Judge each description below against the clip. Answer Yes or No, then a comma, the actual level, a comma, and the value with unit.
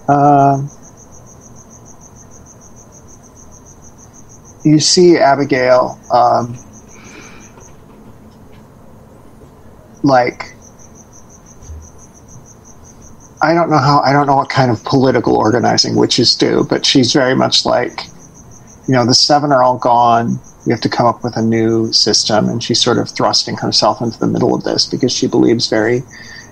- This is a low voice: Yes, low, 125 Hz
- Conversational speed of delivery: No, slow, 125 wpm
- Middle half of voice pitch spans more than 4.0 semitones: No, average, 3.4 semitones